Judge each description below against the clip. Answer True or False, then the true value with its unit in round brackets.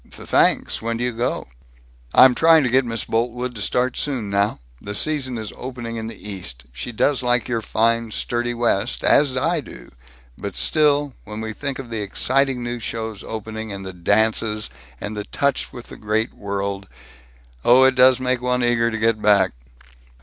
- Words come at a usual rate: True (185 wpm)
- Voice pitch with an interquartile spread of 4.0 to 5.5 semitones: False (2.9 semitones)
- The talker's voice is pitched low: True (115 Hz)